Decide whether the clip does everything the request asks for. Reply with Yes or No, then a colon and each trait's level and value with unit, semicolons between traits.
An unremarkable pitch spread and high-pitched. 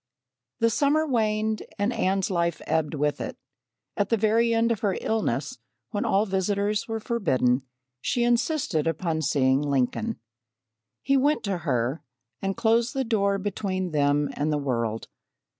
No: wide, 7.3 semitones; high, 195 Hz